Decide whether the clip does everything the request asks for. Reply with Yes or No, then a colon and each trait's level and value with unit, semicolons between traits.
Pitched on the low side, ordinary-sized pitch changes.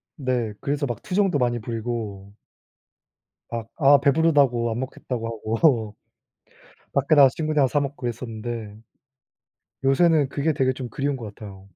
Yes: low, 130 Hz; average, 3.8 semitones